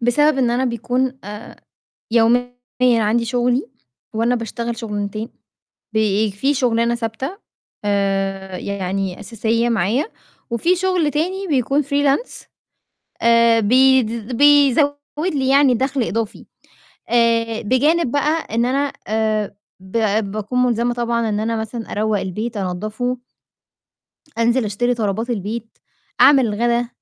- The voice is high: Yes, high, 235 Hz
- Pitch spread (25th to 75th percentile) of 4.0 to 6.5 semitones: No, average, 3.2 semitones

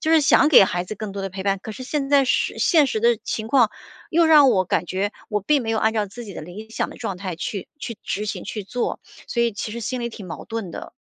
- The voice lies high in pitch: Yes, high, 220 Hz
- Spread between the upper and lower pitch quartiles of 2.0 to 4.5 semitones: Yes, average, 4.2 semitones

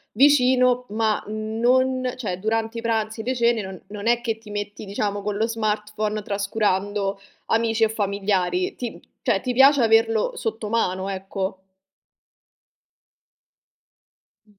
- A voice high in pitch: Yes, high, 215 Hz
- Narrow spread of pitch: Yes, narrow, 2.3 semitones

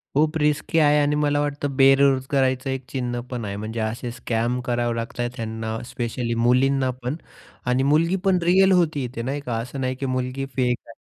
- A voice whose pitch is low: Yes, low, 130 Hz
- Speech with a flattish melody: No, average, 3.3 semitones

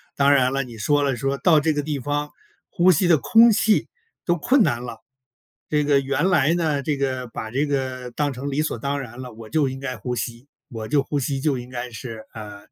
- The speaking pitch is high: No, medium, 140 Hz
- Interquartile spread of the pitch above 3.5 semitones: No, average, 3.2 semitones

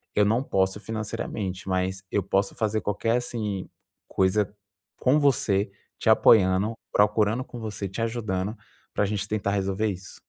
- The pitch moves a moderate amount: No, narrow, 2.3 semitones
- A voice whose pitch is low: Yes, low, 105 Hz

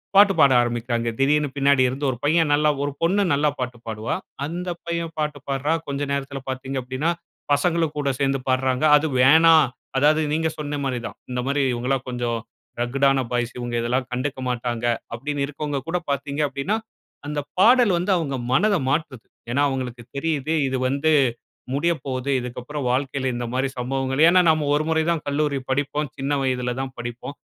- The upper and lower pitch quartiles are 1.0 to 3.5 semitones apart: Yes, average, 2.8 semitones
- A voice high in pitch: No, medium, 140 Hz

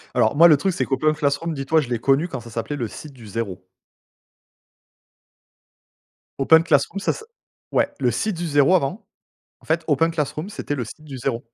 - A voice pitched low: No, medium, 145 Hz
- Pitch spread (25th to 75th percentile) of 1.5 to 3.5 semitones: No, average, 3.9 semitones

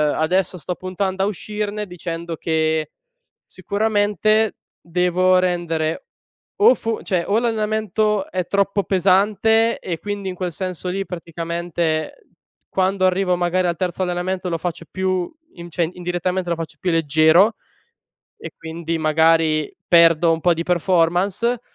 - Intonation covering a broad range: No, average, 2.9 semitones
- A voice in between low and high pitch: Yes, medium, 180 Hz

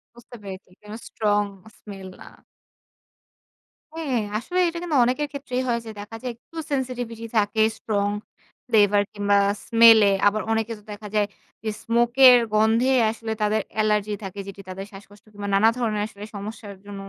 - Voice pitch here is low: No, high, 215 Hz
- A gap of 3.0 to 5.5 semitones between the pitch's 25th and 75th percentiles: No, narrow, 2.6 semitones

